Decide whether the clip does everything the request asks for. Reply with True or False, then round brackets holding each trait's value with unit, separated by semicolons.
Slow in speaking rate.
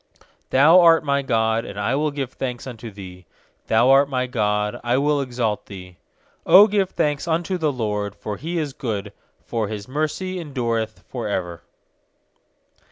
False (165 wpm)